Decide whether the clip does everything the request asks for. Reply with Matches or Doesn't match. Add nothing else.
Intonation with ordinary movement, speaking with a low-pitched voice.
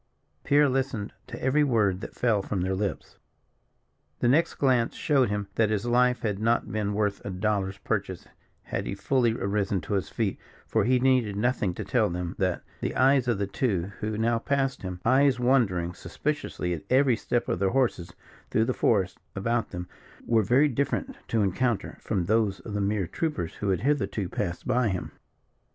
Matches